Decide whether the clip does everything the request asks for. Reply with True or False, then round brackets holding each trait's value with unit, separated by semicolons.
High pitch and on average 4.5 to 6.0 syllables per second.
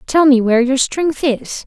True (270 Hz; 4.6 syllables/s)